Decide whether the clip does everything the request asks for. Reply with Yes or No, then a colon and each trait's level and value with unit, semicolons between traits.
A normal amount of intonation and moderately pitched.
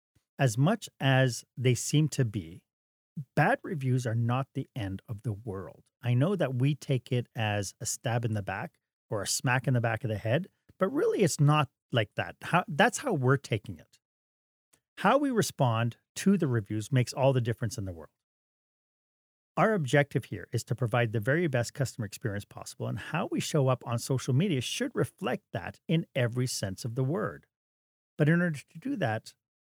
No: average, 4.7 semitones; low, 125 Hz